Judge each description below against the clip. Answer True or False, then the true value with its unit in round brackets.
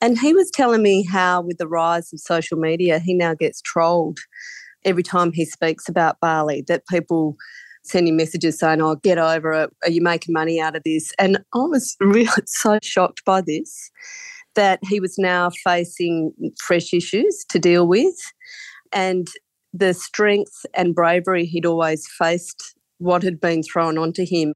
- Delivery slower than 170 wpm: False (175 wpm)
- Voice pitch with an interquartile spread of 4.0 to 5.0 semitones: False (3.0 semitones)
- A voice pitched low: False (175 Hz)